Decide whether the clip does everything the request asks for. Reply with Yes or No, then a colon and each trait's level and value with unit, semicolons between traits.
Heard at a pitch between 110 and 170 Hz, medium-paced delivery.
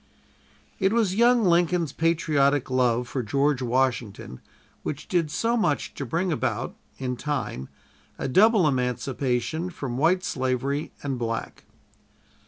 No: medium, 140 Hz; slow, 125 wpm